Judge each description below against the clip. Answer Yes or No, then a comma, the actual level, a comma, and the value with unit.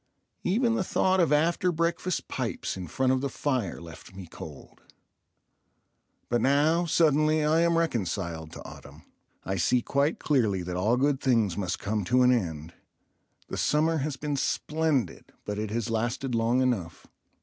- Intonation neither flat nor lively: No, wide, 7.3 semitones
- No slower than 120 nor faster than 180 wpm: Yes, average, 160 wpm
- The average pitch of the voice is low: Yes, low, 130 Hz